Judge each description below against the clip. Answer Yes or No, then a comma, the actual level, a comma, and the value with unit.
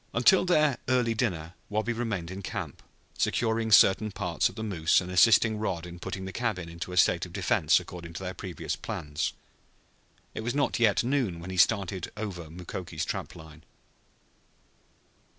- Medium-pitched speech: No, very low, 95 Hz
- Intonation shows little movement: No, average, 4.5 semitones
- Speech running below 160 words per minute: No, average, 170 wpm